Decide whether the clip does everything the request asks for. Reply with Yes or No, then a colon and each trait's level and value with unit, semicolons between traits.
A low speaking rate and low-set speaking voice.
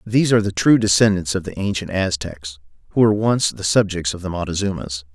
No: average, 200 wpm; very low, 95 Hz